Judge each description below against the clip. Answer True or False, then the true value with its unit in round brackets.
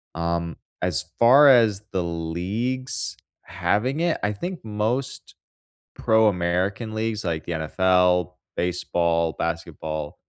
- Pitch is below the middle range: True (95 Hz)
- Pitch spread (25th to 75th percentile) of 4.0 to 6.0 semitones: True (4.9 semitones)